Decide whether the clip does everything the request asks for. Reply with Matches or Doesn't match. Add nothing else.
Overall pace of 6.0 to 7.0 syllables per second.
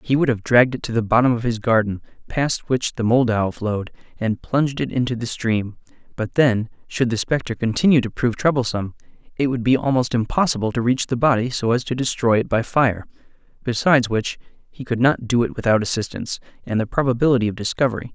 Matches